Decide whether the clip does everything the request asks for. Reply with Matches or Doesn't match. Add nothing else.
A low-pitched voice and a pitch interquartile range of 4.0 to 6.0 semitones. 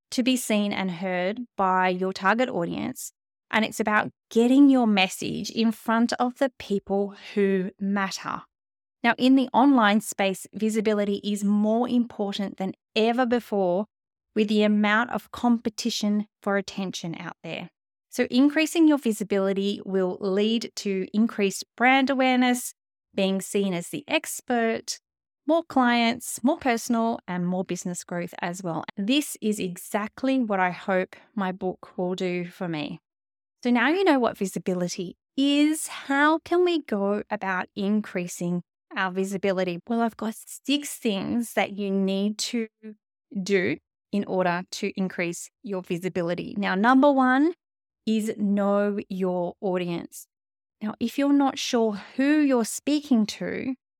Doesn't match